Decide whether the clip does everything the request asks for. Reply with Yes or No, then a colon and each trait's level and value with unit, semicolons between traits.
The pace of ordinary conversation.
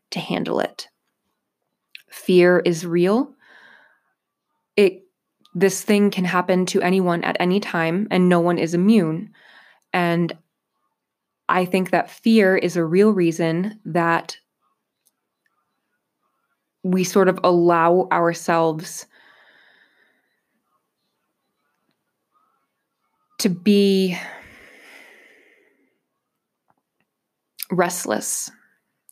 No: slow, 80 wpm